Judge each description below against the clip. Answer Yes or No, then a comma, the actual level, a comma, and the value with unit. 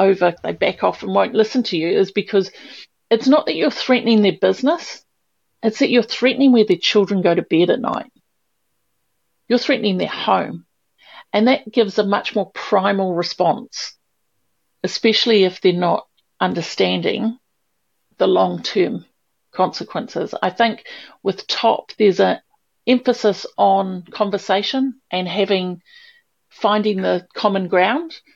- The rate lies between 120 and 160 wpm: Yes, average, 140 wpm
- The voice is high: Yes, high, 210 Hz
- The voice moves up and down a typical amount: Yes, average, 4.2 semitones